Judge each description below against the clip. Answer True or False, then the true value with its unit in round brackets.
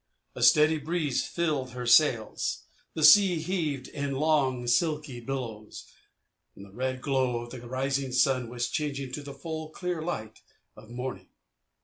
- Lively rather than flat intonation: False (4.0 semitones)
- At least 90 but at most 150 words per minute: True (145 wpm)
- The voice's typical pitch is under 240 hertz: True (135 Hz)